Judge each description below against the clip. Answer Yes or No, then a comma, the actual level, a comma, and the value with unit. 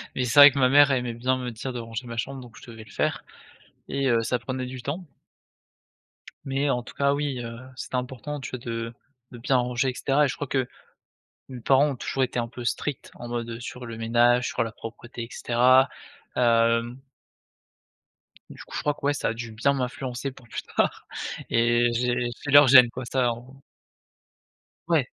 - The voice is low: Yes, low, 125 Hz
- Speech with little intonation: Yes, narrow, 2.2 semitones